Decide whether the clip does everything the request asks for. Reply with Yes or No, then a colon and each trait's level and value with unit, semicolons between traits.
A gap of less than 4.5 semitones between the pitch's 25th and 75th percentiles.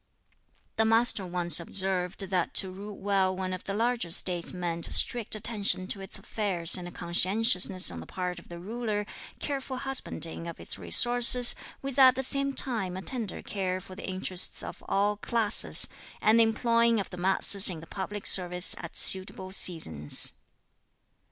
Yes: average, 4.0 semitones